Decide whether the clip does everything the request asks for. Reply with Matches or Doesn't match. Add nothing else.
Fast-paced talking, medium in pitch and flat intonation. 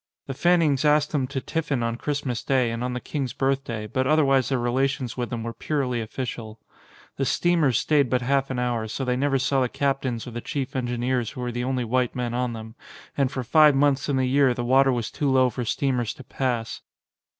Doesn't match